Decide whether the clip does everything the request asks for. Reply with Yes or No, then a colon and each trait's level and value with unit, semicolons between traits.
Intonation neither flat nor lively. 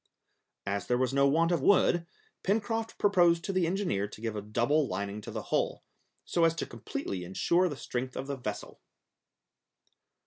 No: wide, 8.3 semitones